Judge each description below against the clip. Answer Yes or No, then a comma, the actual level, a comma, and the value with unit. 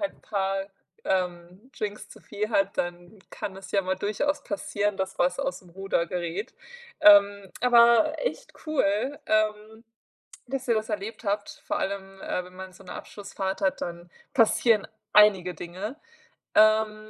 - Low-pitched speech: No, high, 200 Hz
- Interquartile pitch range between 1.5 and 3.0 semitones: Yes, narrow, 2.5 semitones